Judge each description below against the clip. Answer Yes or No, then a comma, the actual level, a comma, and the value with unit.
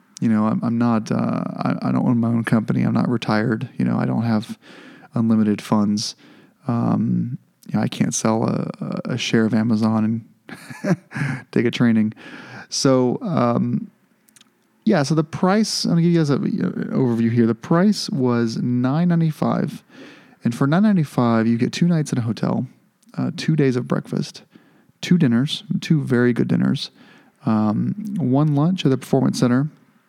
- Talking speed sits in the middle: Yes, average, 170 wpm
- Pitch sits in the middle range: No, low, 125 Hz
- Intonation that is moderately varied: No, wide, 6.6 semitones